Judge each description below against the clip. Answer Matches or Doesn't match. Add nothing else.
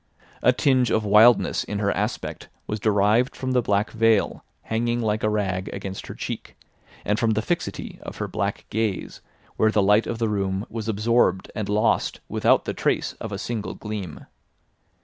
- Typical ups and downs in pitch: Doesn't match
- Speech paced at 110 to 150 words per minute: Doesn't match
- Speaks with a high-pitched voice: Doesn't match